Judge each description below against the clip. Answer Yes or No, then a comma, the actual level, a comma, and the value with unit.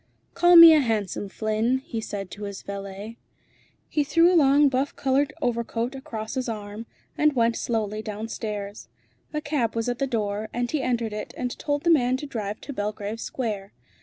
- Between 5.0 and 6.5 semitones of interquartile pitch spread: No, average, 4.5 semitones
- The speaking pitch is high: Yes, high, 230 Hz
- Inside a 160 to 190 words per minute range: Yes, average, 185 wpm